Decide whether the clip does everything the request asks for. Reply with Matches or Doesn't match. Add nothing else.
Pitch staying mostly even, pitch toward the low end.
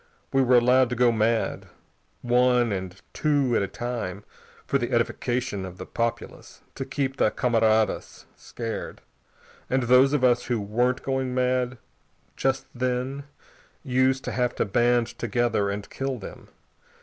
Matches